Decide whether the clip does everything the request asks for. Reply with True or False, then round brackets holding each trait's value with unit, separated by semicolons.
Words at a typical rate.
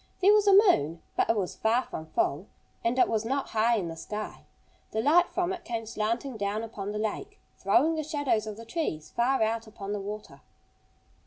False (210 wpm)